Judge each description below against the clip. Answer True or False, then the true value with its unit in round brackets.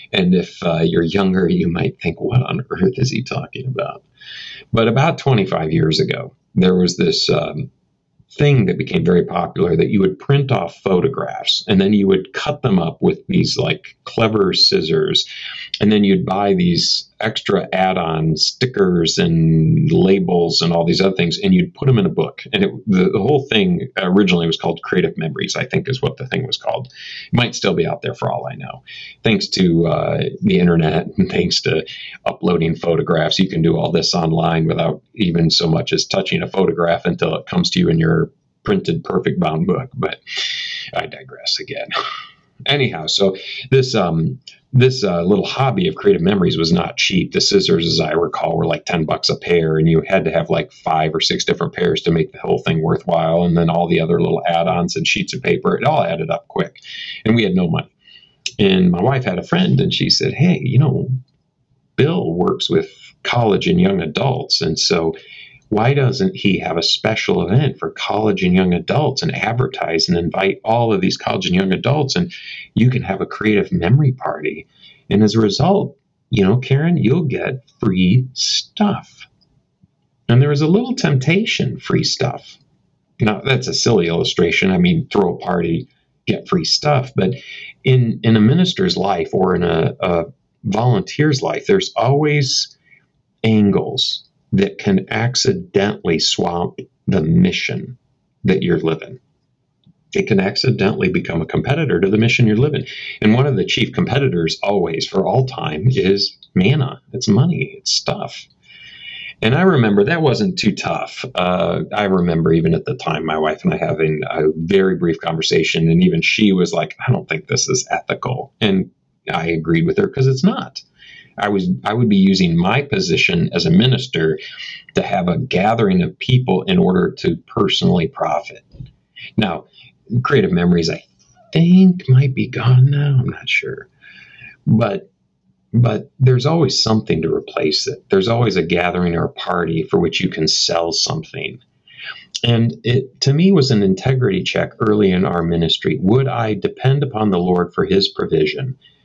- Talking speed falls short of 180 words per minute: False (185 wpm)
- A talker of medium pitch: False (130 Hz)